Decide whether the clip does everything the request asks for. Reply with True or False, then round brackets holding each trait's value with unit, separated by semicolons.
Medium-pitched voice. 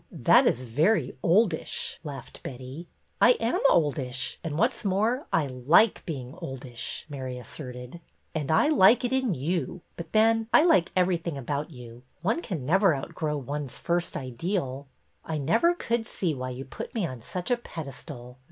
True (160 Hz)